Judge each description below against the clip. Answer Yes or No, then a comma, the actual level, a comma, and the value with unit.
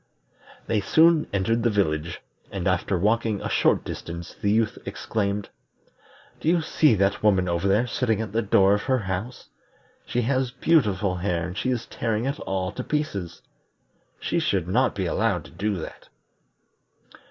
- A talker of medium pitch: No, low, 105 Hz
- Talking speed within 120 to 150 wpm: No, average, 165 wpm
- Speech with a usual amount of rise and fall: Yes, average, 4.2 semitones